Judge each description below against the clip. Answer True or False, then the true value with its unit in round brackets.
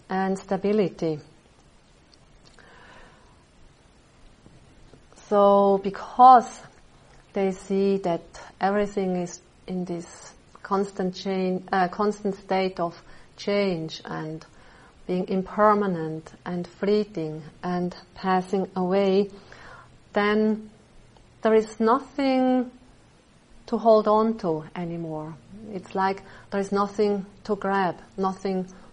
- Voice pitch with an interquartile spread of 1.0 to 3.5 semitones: True (2.6 semitones)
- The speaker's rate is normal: False (90 wpm)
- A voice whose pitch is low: False (195 Hz)